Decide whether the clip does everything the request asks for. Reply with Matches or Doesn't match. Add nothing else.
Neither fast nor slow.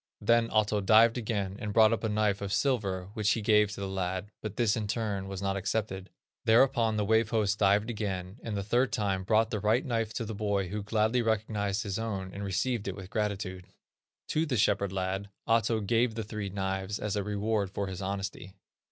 Doesn't match